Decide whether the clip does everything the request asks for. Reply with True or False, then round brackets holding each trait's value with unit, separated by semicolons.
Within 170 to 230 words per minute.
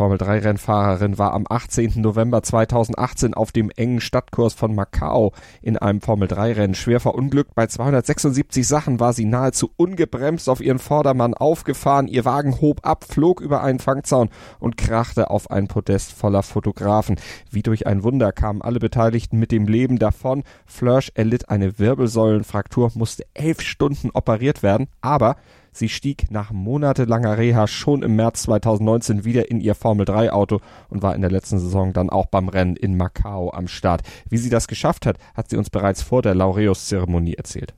True (175 wpm)